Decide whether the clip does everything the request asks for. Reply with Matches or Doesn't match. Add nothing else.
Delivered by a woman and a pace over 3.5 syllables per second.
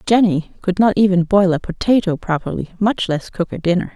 Matches